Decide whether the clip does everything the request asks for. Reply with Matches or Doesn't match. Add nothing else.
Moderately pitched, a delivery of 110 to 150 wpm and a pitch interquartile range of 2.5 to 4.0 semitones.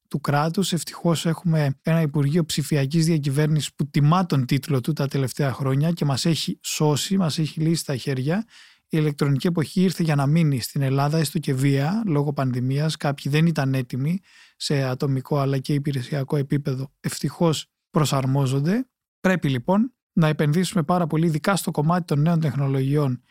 Doesn't match